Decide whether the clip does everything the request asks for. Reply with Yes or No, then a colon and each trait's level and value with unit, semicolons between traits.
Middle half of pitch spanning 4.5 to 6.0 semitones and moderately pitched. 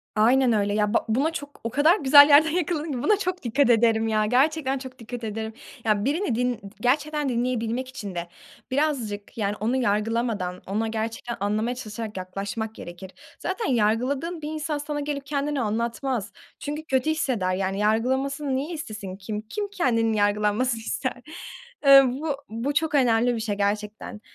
No: average, 5.0 semitones; high, 240 Hz